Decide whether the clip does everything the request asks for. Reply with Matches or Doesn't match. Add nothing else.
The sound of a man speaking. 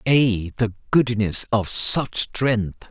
Matches